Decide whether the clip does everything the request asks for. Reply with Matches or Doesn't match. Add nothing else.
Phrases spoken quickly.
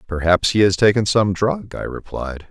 Doesn't match